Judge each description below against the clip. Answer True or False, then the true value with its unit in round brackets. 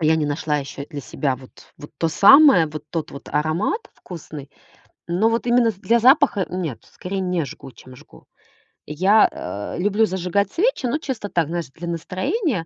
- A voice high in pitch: False (175 Hz)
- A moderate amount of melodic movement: False (6.5 semitones)